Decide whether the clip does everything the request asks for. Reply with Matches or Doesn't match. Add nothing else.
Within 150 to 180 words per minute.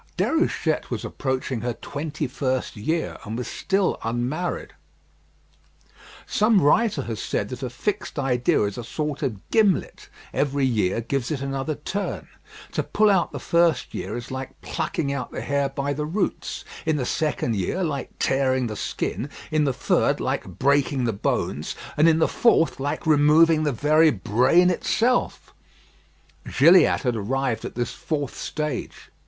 Matches